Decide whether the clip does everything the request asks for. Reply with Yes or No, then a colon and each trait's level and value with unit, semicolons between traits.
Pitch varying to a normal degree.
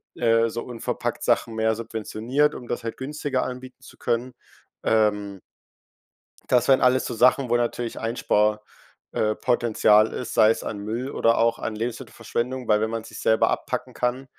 No: narrow, 2.2 semitones